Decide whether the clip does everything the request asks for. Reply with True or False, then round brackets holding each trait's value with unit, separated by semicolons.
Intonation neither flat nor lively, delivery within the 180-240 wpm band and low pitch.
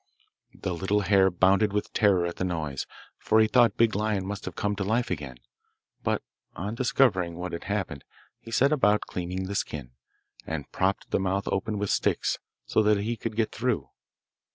True (3.2 semitones; 185 wpm; 100 Hz)